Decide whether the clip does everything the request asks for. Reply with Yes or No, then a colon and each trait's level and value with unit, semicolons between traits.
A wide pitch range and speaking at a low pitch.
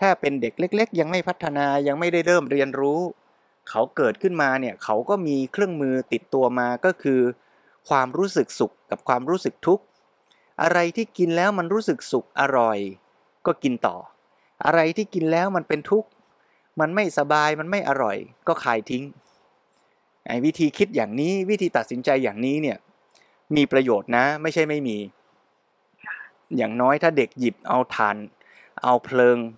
No: wide, 5.9 semitones; medium, 150 Hz